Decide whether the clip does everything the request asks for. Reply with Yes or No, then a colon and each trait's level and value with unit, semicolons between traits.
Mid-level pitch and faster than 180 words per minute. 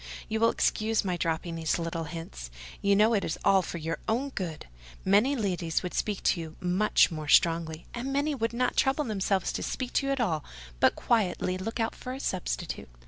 No: high, 195 Hz; average, 195 wpm